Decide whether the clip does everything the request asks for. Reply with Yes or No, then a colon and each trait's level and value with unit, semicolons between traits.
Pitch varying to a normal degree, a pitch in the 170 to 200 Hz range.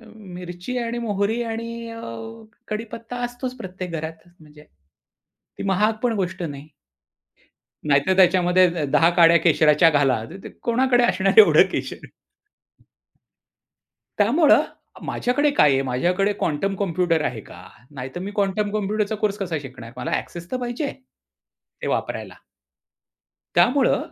No: wide, 5.8 semitones; high, 190 Hz